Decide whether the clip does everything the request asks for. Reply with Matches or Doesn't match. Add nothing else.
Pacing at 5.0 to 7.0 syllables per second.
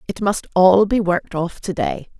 Doesn't match